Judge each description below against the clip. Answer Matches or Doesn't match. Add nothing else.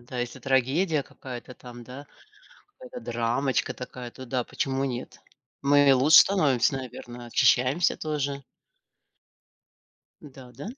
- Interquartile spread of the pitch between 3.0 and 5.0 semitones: Doesn't match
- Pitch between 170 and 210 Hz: Doesn't match